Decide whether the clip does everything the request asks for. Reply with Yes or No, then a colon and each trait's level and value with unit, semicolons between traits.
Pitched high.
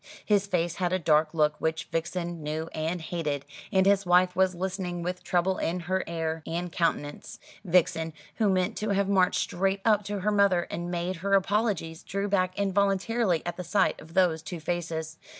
No: medium, 180 Hz